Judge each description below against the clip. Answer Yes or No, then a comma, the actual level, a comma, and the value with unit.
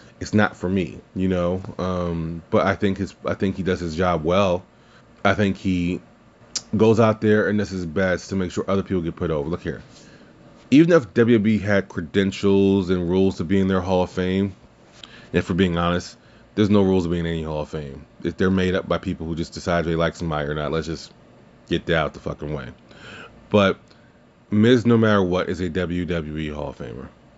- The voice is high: No, very low, 95 Hz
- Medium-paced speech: No, fast, 215 wpm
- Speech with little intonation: No, average, 3.0 semitones